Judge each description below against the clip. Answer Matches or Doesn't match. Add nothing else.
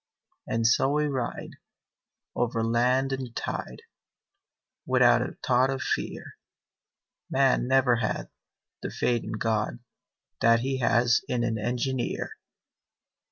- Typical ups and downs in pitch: Doesn't match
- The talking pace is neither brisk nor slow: Doesn't match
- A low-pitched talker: Matches